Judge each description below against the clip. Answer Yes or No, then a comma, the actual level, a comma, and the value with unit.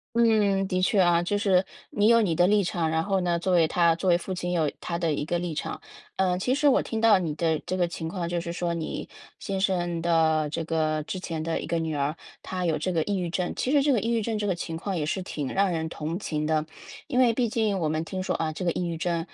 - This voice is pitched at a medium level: Yes, medium, 175 Hz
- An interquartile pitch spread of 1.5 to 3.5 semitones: Yes, average, 3.1 semitones